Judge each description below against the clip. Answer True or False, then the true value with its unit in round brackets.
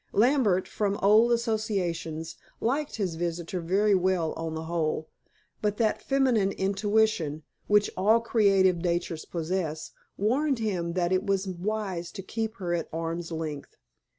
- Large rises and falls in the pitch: False (4.2 semitones)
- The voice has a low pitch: False (190 Hz)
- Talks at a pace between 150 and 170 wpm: False (140 wpm)